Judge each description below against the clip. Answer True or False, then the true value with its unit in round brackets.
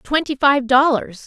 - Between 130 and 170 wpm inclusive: True (140 wpm)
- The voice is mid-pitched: False (270 Hz)